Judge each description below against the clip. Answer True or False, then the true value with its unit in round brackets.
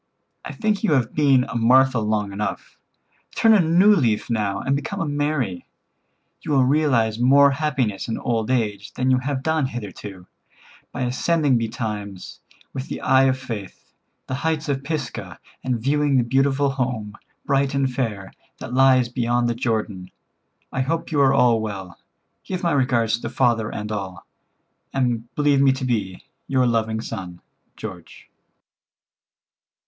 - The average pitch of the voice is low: True (125 Hz)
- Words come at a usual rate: True (155 wpm)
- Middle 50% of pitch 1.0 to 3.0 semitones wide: False (4.0 semitones)